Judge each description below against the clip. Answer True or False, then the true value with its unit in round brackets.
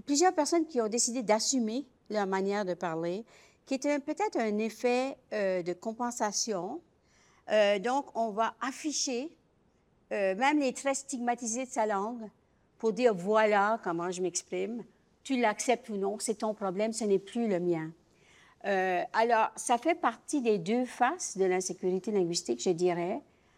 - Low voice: False (220 Hz)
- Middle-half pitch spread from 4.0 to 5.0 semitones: True (4.6 semitones)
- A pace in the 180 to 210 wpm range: False (160 wpm)